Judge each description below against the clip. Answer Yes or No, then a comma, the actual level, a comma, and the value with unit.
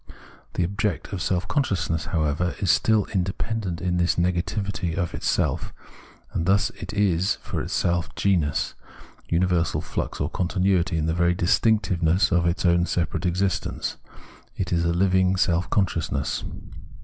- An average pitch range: No, narrow, 2.1 semitones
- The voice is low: Yes, very low, 90 Hz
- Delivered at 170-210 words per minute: No, average, 140 wpm